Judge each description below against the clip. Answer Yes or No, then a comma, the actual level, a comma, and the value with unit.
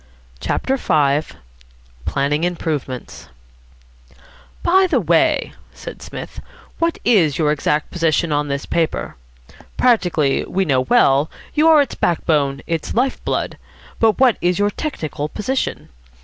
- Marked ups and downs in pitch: Yes, wide, 8.0 semitones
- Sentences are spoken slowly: Yes, slow, 130 wpm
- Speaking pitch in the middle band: Yes, medium, 165 Hz